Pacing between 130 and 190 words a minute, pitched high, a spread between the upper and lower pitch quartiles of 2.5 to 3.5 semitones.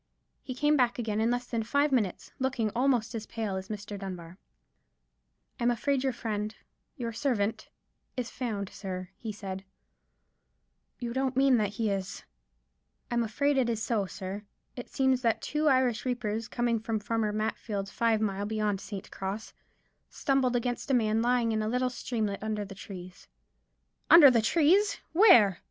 Yes: average, 160 wpm; high, 225 Hz; average, 3.2 semitones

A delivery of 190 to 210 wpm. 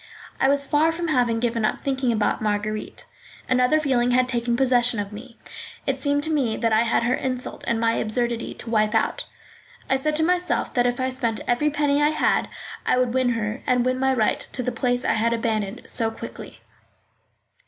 Yes: fast, 205 wpm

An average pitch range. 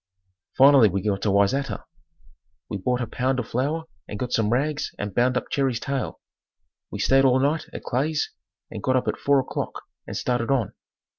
Yes: average, 3.4 semitones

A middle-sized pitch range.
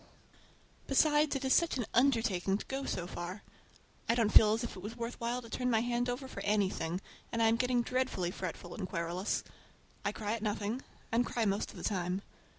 Yes: average, 4.0 semitones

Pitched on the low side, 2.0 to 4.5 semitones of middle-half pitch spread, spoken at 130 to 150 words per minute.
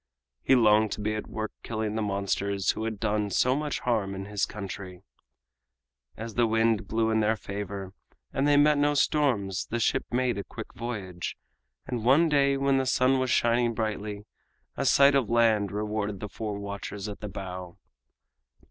No: low, 110 Hz; average, 3.5 semitones; average, 180 wpm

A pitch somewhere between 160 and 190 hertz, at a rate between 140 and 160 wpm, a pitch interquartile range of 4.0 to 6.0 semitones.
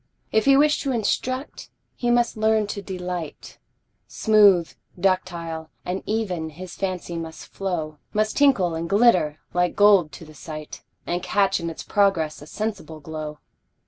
Yes: medium, 185 Hz; average, 150 wpm; average, 4.8 semitones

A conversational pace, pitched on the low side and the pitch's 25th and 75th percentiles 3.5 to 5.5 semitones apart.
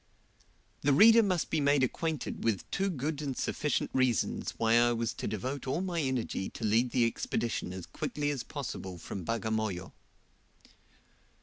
Yes: average, 160 wpm; low, 130 Hz; average, 4.7 semitones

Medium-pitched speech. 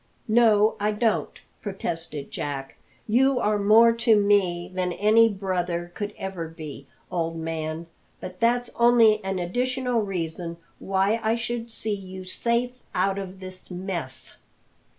No: high, 195 Hz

